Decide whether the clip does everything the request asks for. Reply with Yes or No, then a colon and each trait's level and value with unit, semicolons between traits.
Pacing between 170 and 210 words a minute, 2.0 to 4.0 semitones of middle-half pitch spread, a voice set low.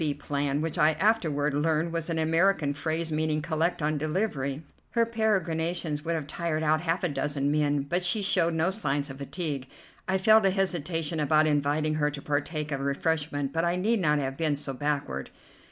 No: average, 190 wpm; average, 2.7 semitones; medium, 155 Hz